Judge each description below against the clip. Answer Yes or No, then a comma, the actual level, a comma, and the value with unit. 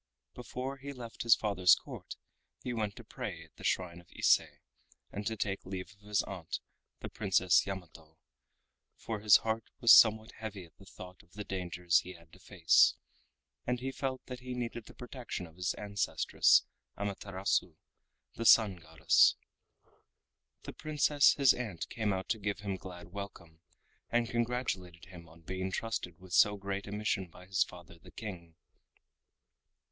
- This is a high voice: No, low, 100 Hz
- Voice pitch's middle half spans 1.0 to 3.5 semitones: No, average, 4.1 semitones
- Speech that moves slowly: No, average, 165 wpm